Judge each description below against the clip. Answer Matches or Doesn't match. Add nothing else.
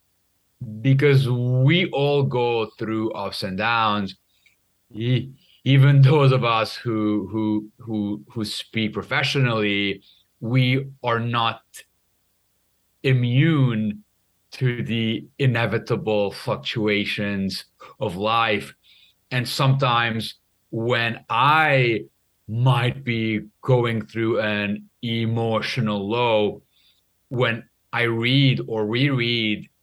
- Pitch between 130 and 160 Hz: Doesn't match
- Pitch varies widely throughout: Doesn't match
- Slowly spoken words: Matches